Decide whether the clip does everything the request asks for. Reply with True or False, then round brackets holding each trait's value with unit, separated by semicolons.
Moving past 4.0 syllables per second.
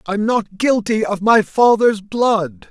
False (3.5 syllables/s)